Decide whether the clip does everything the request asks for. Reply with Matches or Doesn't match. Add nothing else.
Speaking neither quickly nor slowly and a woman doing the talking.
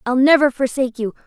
Matches